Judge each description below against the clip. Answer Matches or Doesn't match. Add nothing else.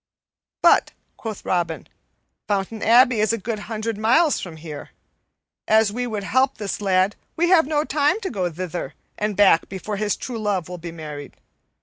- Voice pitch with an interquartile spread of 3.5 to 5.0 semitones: Matches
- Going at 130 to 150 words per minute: Doesn't match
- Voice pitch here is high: Matches